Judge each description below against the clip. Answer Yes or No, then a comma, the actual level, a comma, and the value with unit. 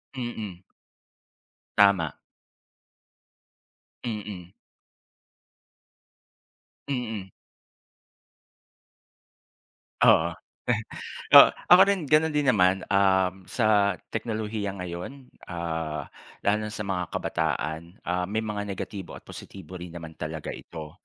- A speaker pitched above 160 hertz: No, low, 100 Hz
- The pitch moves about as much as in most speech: Yes, average, 3.9 semitones